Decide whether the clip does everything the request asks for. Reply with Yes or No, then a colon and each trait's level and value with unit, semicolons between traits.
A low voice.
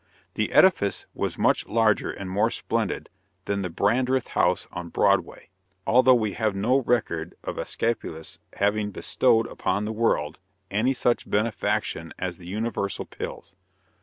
Yes: low, 105 Hz